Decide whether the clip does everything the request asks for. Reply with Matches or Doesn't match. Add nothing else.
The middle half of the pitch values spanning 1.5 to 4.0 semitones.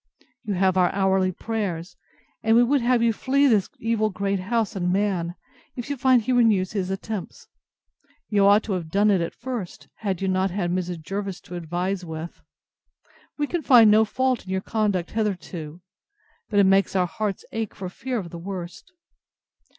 Matches